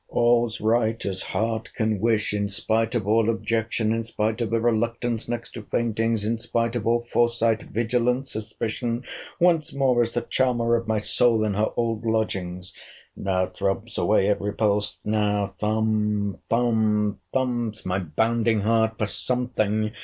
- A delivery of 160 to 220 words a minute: No, average, 145 wpm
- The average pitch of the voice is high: No, low, 110 Hz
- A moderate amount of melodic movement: No, narrow, 1.8 semitones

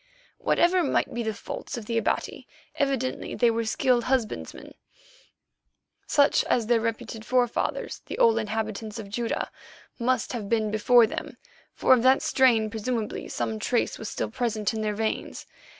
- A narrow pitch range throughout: Yes, narrow, 2.2 semitones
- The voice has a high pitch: Yes, high, 230 Hz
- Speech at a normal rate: Yes, average, 155 wpm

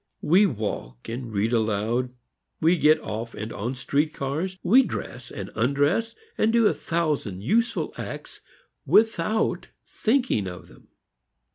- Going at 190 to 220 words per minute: No, slow, 135 wpm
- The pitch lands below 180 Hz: Yes, medium, 140 Hz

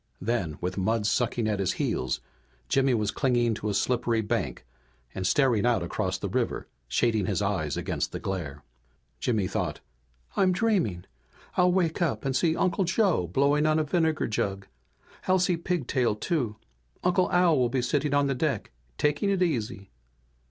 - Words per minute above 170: No, average, 165 wpm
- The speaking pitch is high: No, low, 125 Hz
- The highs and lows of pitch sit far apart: Yes, wide, 7.8 semitones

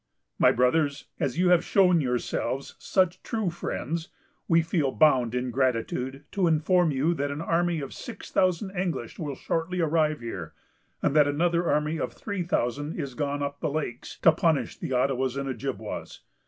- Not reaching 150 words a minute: No, average, 170 wpm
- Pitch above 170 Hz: No, medium, 150 Hz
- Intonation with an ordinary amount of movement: Yes, average, 4.1 semitones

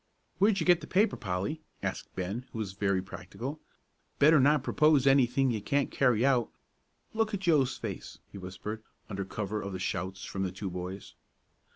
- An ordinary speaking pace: Yes, average, 180 wpm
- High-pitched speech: No, low, 120 Hz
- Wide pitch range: Yes, wide, 7.1 semitones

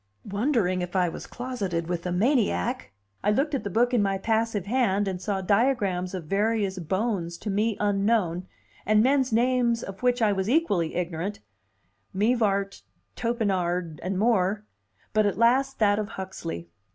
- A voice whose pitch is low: No, high, 205 Hz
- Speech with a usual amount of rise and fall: Yes, average, 4.0 semitones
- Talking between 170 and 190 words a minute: No, average, 160 wpm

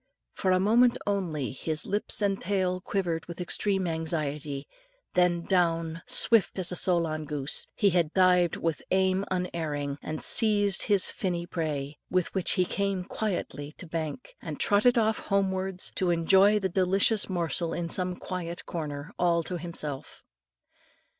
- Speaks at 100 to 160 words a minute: Yes, average, 145 wpm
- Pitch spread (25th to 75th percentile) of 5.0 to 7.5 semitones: No, average, 2.9 semitones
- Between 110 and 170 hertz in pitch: No, medium, 180 Hz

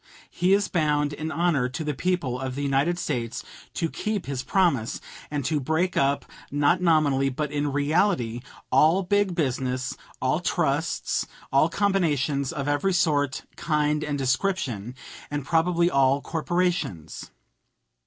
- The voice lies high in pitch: No, medium, 150 Hz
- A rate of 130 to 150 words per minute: Yes, average, 140 wpm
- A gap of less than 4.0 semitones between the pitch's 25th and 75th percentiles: No, average, 4.3 semitones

